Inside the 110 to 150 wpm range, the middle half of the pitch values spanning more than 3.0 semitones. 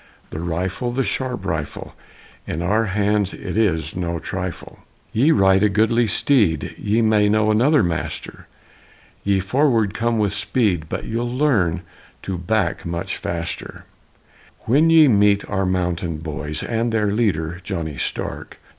Yes: average, 145 wpm; average, 4.5 semitones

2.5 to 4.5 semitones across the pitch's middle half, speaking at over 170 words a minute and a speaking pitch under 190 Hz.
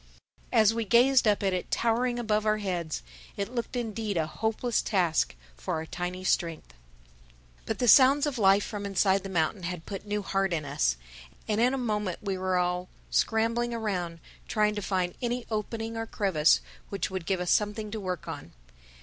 No: average, 3.8 semitones; average, 185 wpm; high, 205 Hz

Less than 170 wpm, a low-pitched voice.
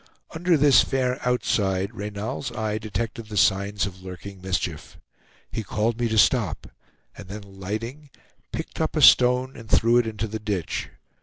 Yes: average, 160 wpm; low, 110 Hz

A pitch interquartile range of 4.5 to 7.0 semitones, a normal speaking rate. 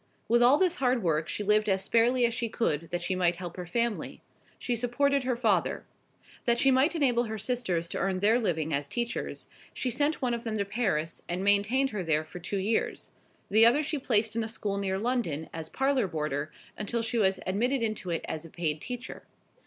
No: wide, 5.4 semitones; fast, 215 wpm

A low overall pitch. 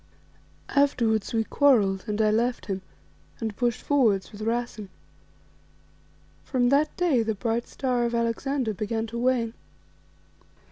No: high, 235 Hz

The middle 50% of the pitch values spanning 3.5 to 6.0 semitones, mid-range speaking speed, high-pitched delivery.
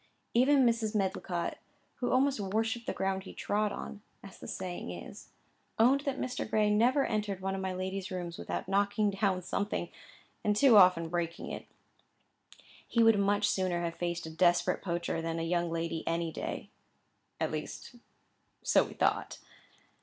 Yes: average, 3.8 semitones; average, 165 wpm; high, 195 Hz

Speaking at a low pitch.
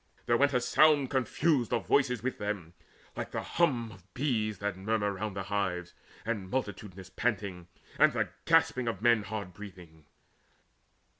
Yes: low, 105 Hz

